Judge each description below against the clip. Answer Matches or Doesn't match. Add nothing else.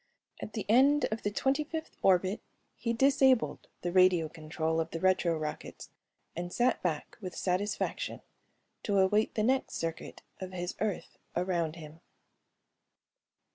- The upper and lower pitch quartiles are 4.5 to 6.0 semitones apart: Matches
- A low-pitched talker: Doesn't match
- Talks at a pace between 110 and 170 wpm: Matches